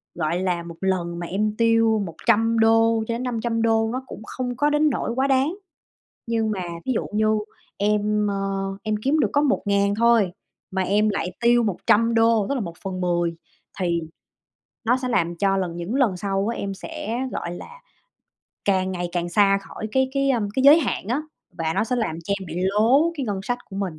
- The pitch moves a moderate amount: Yes, average, 3.9 semitones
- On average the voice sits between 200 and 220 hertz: Yes, high, 215 Hz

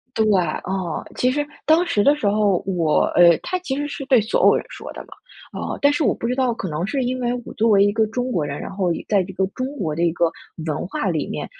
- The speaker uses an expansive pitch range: Yes, wide, 6.4 semitones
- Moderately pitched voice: No, high, 215 Hz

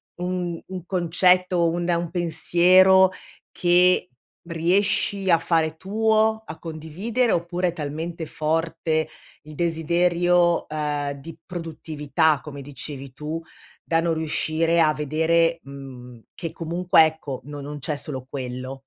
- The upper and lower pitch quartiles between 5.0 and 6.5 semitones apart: No, average, 2.7 semitones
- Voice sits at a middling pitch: Yes, medium, 165 Hz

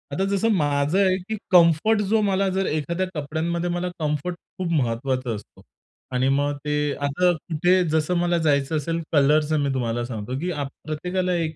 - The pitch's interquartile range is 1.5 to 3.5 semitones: No, average, 4.1 semitones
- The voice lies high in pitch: No, medium, 160 Hz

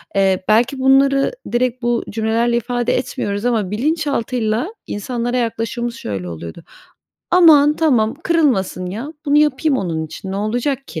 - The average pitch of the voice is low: No, high, 240 Hz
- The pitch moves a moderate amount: Yes, average, 4.6 semitones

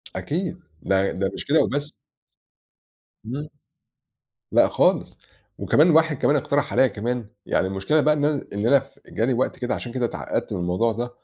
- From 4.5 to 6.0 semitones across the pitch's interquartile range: Yes, average, 4.8 semitones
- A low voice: Yes, low, 130 Hz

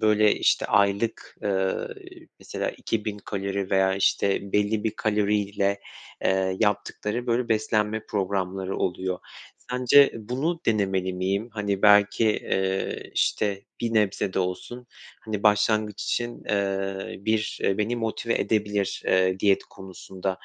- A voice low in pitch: Yes, low, 105 Hz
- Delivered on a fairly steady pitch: Yes, narrow, 2.1 semitones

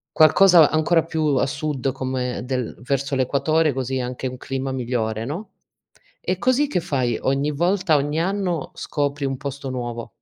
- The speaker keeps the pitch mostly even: No, average, 3.7 semitones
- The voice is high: No, medium, 140 Hz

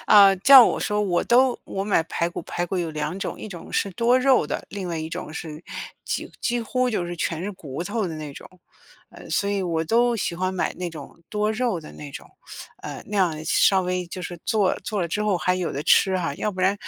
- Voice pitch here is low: No, medium, 185 Hz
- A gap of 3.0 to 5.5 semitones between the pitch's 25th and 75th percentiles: Yes, average, 3.7 semitones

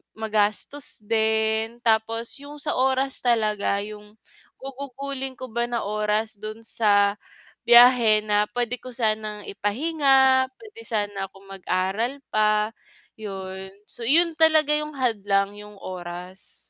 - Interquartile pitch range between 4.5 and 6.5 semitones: No, average, 4.0 semitones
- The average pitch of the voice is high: Yes, high, 220 Hz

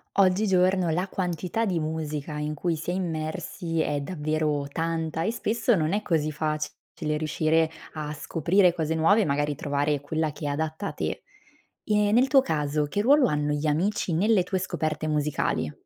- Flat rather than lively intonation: No, average, 3.6 semitones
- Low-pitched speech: No, medium, 160 Hz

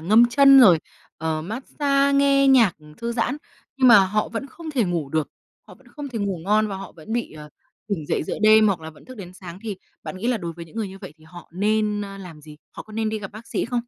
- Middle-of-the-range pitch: No, high, 210 Hz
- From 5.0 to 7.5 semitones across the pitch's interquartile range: Yes, wide, 5.4 semitones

